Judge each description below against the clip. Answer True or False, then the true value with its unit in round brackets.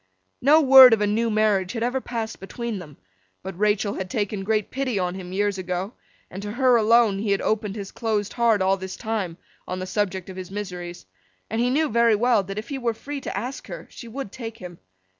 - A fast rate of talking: True (225 wpm)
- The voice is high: True (210 Hz)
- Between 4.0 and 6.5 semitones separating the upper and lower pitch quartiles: False (3.5 semitones)